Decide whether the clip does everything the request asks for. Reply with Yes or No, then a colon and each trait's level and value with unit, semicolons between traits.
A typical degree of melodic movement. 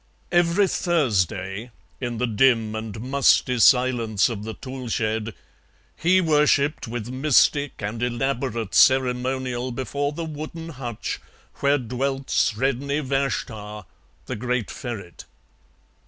Yes: average, 3.8 semitones